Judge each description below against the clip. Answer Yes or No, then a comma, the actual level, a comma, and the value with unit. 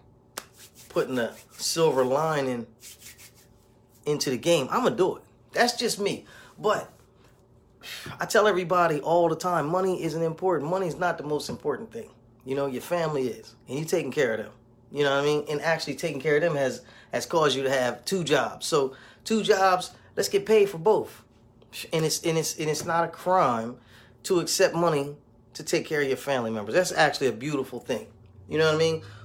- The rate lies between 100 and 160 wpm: No, average, 200 wpm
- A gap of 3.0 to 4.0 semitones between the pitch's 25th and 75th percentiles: No, average, 5.1 semitones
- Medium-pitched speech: Yes, medium, 155 Hz